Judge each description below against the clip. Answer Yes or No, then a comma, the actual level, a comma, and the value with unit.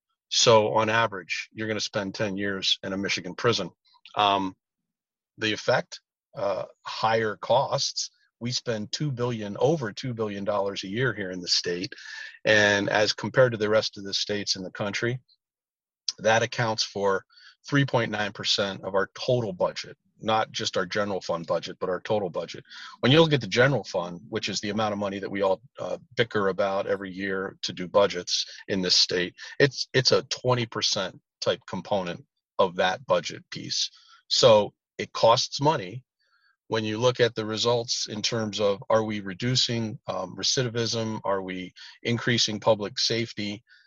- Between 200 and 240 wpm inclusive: No, average, 170 wpm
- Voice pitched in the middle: No, low, 110 Hz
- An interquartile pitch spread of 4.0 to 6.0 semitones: No, average, 3.1 semitones